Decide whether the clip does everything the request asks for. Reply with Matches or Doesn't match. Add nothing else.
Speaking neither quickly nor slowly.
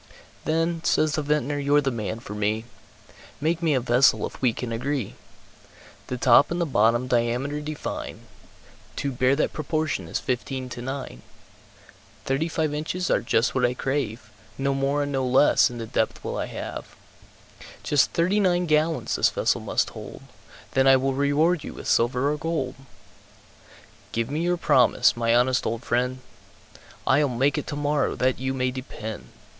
Matches